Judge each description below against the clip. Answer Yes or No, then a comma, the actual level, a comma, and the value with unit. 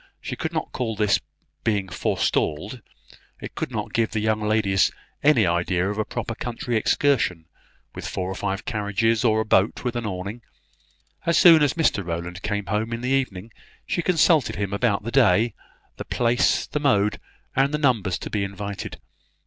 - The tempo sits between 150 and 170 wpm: No, average, 180 wpm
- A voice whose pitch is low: Yes, low, 110 Hz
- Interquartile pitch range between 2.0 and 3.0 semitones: No, average, 3.7 semitones